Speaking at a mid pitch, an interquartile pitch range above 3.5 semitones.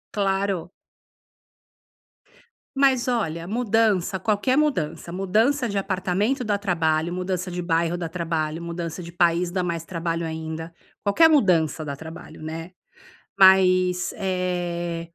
No: medium, 180 Hz; average, 3.1 semitones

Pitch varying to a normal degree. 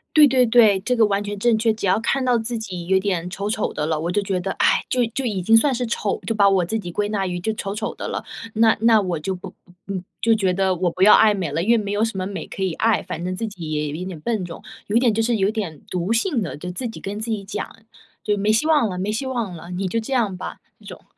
Yes: average, 3.5 semitones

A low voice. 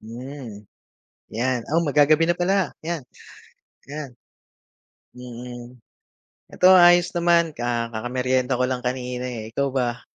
Yes: low, 130 Hz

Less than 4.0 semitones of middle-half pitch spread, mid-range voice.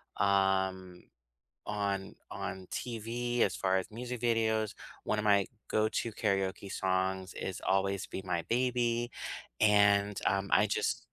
No: average, 2.8 semitones; low, 100 Hz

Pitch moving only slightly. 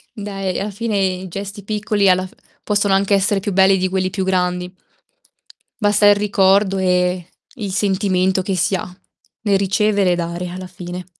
Yes: narrow, 1.8 semitones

